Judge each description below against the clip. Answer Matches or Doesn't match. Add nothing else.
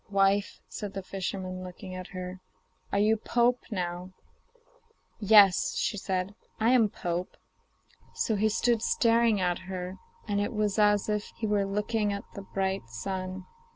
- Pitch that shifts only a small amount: Matches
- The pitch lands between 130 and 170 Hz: Doesn't match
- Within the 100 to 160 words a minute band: Matches